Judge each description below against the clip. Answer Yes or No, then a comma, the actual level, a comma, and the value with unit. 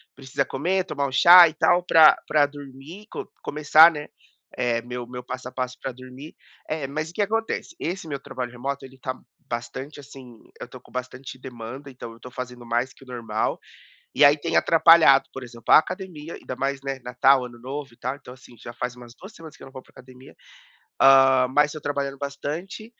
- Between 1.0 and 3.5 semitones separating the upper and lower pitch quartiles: Yes, average, 3.1 semitones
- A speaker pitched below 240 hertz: Yes, low, 135 Hz